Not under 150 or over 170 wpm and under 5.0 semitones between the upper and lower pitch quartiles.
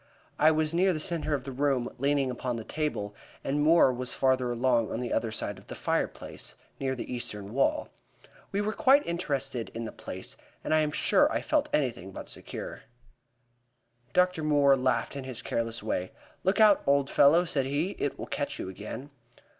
No: average, 190 wpm; average, 4.3 semitones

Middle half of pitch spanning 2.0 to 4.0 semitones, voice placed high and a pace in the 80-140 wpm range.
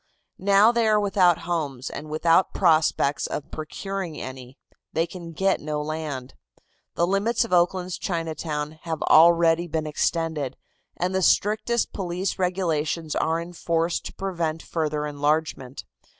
No: average, 3.1 semitones; medium, 165 Hz; slow, 135 wpm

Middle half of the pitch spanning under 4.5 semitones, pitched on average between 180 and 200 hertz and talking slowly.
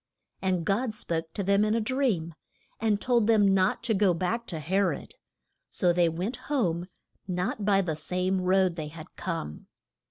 No: average, 3.8 semitones; high, 190 Hz; average, 180 wpm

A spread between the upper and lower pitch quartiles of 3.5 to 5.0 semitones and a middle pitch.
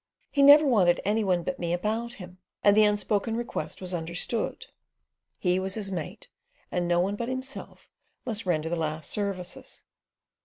No: average, 4.0 semitones; high, 195 Hz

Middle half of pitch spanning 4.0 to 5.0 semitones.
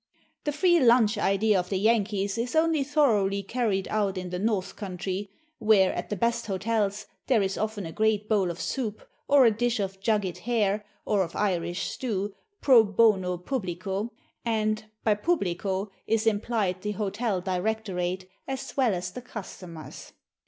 No: average, 3.2 semitones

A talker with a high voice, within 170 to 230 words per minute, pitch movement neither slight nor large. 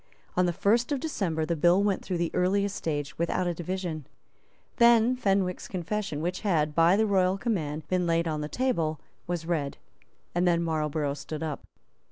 No: medium, 175 Hz; average, 180 wpm; average, 3.8 semitones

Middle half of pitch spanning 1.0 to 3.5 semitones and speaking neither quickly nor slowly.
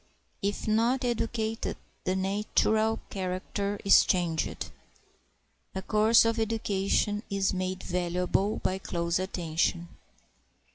No: average, 3.0 semitones; slow, 100 wpm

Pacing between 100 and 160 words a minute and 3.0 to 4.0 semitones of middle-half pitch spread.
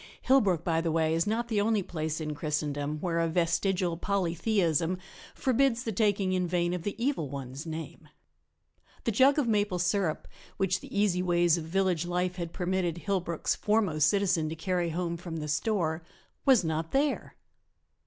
No: average, 170 wpm; average, 3.7 semitones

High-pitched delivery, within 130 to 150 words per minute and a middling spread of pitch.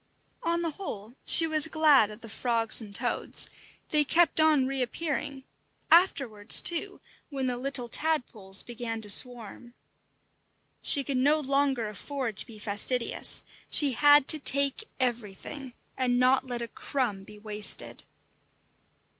Yes: very high, 255 Hz; average, 140 wpm; average, 4.2 semitones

